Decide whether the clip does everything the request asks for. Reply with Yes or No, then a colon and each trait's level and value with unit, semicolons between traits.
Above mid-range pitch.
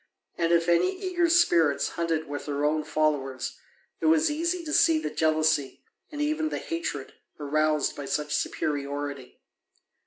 No: medium, 155 Hz